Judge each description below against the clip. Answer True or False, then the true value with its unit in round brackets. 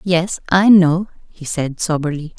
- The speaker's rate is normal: True (150 wpm)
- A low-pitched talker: False (170 Hz)